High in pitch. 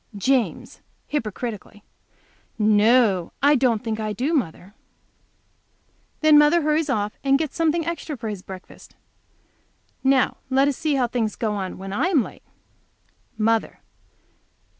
Yes: high, 245 Hz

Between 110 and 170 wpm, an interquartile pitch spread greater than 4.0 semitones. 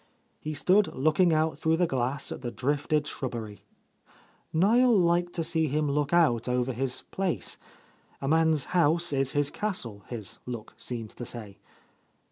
Yes: average, 160 wpm; average, 5.2 semitones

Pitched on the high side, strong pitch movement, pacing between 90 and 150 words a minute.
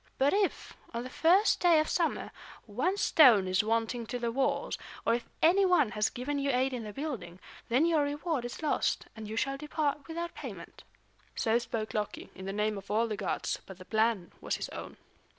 No: high, 245 Hz; wide, 6.0 semitones; fast, 205 wpm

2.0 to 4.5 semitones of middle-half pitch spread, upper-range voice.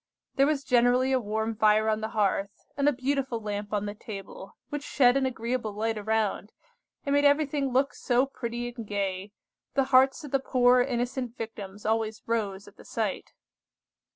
Yes: average, 3.8 semitones; high, 235 Hz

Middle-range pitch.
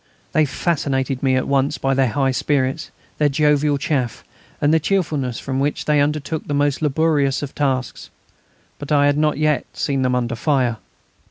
Yes: medium, 145 Hz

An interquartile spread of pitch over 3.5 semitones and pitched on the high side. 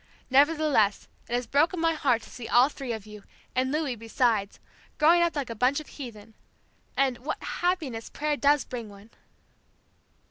Yes: average, 4.8 semitones; very high, 260 Hz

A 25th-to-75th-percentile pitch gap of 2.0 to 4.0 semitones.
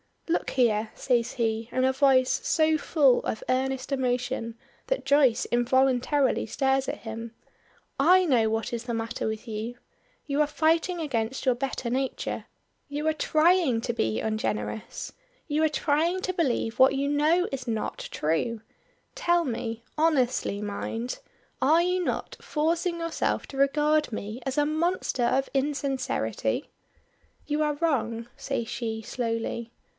No: average, 4.7 semitones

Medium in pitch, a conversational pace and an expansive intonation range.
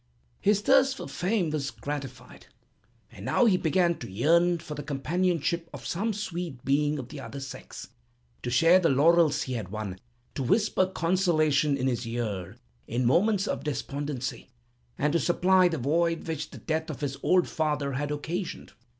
No: medium, 155 Hz; average, 170 wpm; average, 4.5 semitones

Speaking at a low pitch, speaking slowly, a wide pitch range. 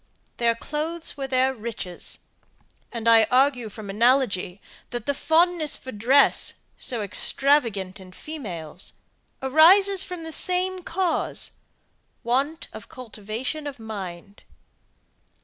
No: very high, 255 Hz; slow, 115 wpm; wide, 6.3 semitones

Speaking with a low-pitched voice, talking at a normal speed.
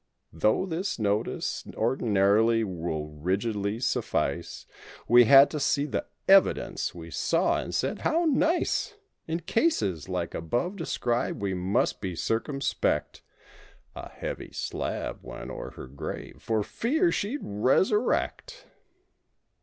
No: low, 115 Hz; slow, 120 wpm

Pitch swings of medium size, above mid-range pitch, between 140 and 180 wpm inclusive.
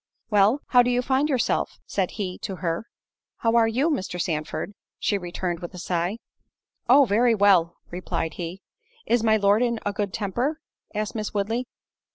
Yes: average, 4.7 semitones; high, 205 Hz; average, 170 wpm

